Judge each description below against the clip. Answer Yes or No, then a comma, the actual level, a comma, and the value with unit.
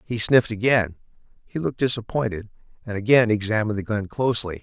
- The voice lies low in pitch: Yes, low, 110 Hz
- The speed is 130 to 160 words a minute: Yes, average, 155 wpm